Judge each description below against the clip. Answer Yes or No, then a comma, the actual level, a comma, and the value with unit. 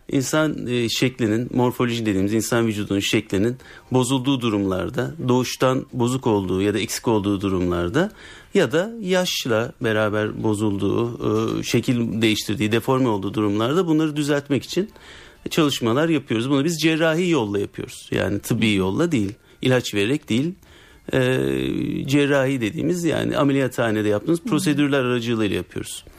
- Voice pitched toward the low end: Yes, low, 120 Hz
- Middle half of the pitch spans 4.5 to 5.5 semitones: Yes, average, 5.1 semitones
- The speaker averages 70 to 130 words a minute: Yes, average, 120 wpm